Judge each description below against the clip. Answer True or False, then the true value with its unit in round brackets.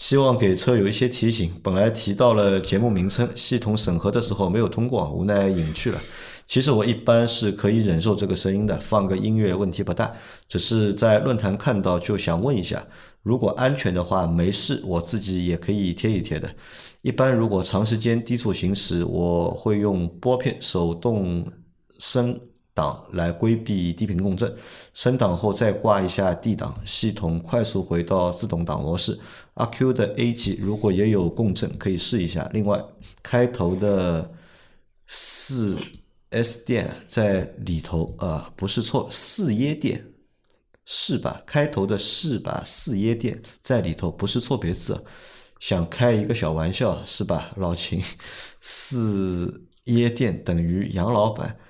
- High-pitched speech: False (105 Hz)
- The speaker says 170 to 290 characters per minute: True (240 characters per minute)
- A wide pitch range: False (4.3 semitones)